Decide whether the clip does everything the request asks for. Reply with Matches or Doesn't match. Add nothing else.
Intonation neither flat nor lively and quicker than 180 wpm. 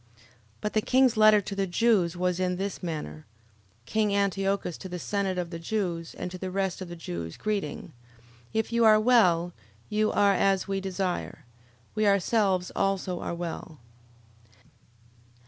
Doesn't match